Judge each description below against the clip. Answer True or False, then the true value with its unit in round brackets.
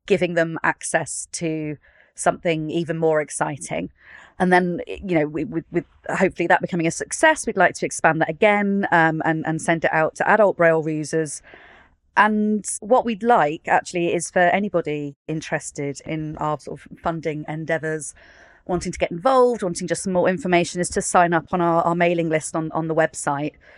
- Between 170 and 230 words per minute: True (180 wpm)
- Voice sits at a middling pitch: True (170 Hz)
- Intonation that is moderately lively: False (2.3 semitones)